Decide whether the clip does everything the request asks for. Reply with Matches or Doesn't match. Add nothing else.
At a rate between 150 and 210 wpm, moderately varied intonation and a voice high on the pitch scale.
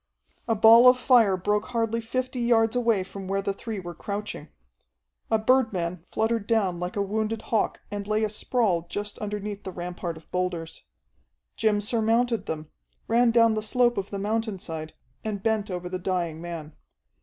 Matches